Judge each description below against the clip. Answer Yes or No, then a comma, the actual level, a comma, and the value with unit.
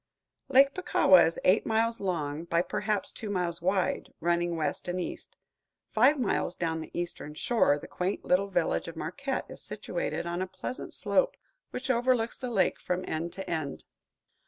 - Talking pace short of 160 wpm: No, average, 170 wpm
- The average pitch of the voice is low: No, medium, 185 Hz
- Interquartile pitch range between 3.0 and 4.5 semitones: No, average, 5.1 semitones